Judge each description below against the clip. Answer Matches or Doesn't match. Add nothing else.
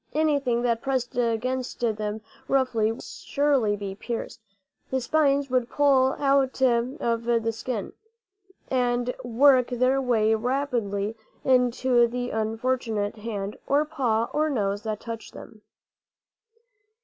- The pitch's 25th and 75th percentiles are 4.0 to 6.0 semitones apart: Doesn't match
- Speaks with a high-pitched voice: Matches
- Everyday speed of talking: Doesn't match